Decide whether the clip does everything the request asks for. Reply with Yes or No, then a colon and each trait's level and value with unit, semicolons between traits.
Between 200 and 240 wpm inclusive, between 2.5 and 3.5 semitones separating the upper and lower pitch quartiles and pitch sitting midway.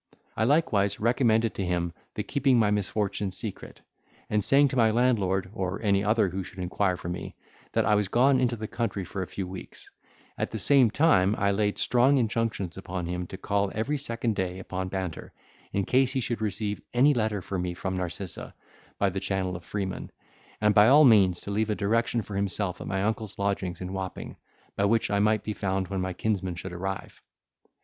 No: fast, 205 wpm; average, 3.2 semitones; low, 100 Hz